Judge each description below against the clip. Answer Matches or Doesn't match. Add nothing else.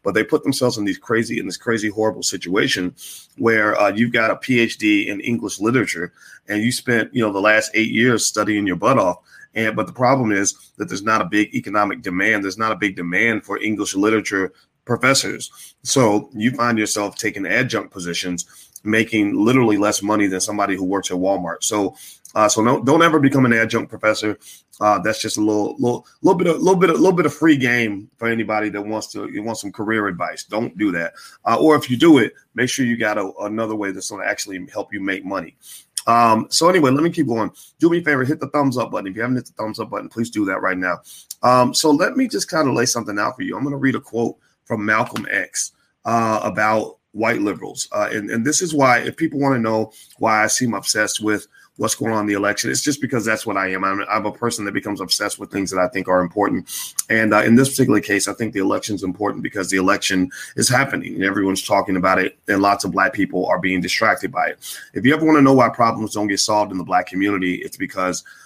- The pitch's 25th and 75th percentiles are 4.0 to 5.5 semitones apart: Doesn't match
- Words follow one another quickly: Matches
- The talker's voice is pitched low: Matches